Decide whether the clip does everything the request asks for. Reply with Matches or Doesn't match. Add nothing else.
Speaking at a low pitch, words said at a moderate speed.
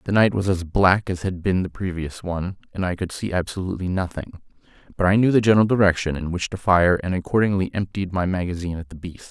Doesn't match